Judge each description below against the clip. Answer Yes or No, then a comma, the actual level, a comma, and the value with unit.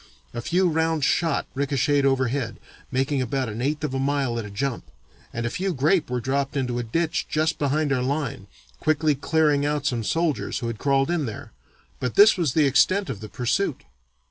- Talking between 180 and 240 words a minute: Yes, average, 195 wpm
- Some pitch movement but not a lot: Yes, average, 3.8 semitones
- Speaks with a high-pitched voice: No, medium, 140 Hz